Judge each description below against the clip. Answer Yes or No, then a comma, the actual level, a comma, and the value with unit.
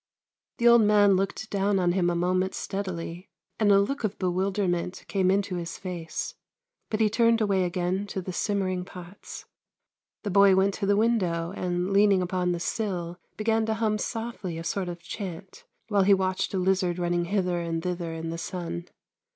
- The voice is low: No, high, 190 Hz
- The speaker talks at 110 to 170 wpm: No, average, 185 wpm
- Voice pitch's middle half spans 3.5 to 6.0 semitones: No, narrow, 2.5 semitones